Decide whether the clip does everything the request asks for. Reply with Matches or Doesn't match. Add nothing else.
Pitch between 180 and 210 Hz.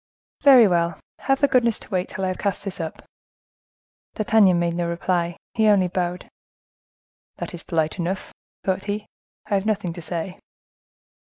Matches